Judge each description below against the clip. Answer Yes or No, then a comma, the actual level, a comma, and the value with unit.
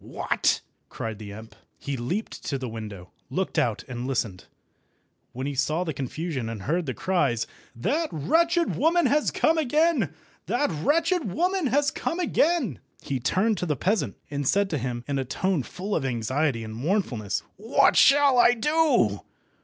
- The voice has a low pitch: No, medium, 160 Hz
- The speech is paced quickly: No, average, 165 wpm